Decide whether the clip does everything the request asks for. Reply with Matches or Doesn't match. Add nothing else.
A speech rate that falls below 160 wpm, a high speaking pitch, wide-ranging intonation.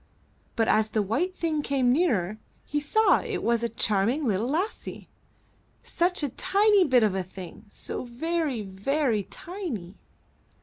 Matches